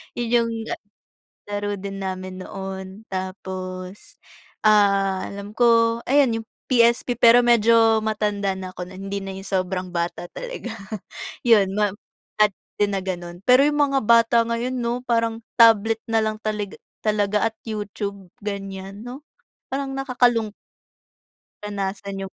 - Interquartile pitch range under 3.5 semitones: Yes, average, 3.1 semitones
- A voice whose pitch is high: Yes, high, 210 Hz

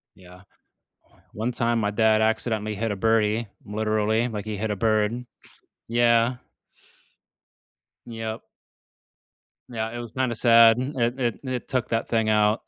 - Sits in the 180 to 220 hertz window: No, low, 115 Hz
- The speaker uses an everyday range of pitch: No, narrow, 1.7 semitones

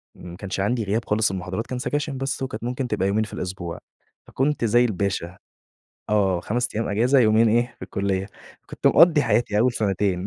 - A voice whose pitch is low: Yes, low, 110 Hz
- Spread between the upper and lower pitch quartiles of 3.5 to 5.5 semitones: Yes, average, 4.0 semitones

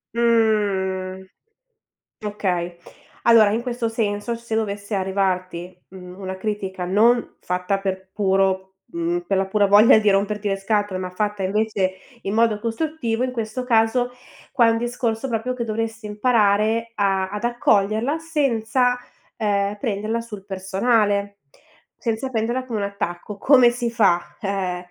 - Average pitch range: Yes, average, 3.1 semitones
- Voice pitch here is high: Yes, high, 210 Hz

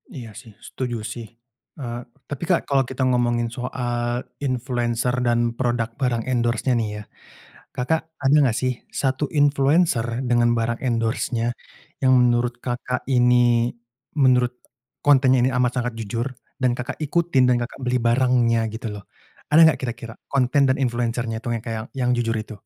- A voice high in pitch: No, low, 125 Hz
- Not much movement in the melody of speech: Yes, narrow, 1.7 semitones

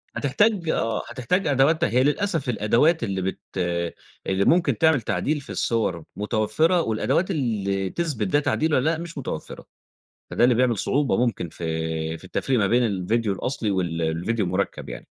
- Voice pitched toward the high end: No, low, 115 Hz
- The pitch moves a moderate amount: No, wide, 7.7 semitones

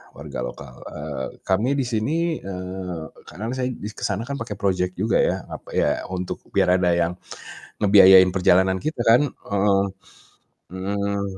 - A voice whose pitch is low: Yes, low, 100 Hz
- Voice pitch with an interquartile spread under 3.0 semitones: No, average, 3.5 semitones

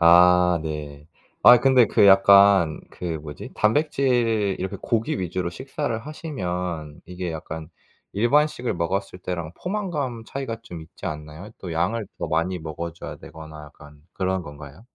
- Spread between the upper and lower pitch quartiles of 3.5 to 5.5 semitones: No, wide, 6.0 semitones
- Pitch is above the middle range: No, very low, 90 Hz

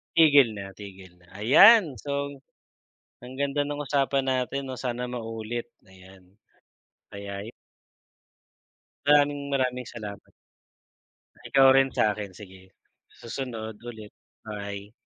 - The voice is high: No, low, 120 Hz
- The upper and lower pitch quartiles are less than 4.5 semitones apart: No, average, 5.2 semitones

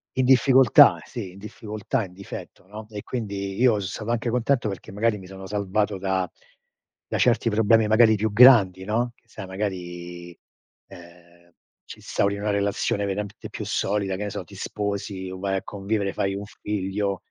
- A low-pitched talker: Yes, low, 100 Hz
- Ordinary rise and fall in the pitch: No, narrow, 2.3 semitones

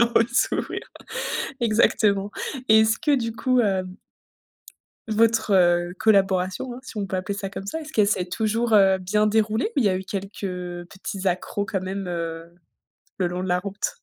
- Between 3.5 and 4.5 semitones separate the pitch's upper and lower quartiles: No, average, 2.9 semitones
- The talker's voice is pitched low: No, high, 200 Hz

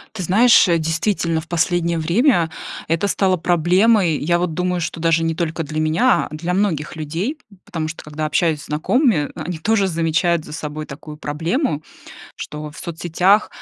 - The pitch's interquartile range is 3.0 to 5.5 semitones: No, narrow, 2.6 semitones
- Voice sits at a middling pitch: Yes, medium, 165 Hz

